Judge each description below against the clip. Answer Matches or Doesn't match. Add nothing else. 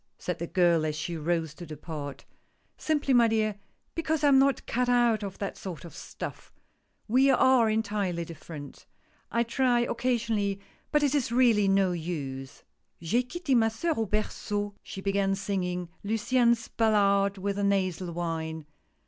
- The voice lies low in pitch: Doesn't match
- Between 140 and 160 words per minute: Doesn't match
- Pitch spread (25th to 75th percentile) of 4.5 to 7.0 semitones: Matches